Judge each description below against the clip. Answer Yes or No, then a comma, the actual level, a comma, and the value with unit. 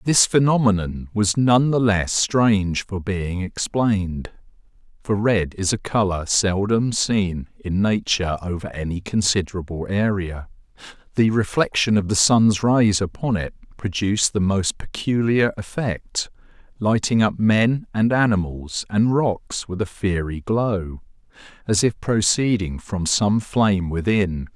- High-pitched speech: No, low, 100 Hz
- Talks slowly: Yes, slow, 130 wpm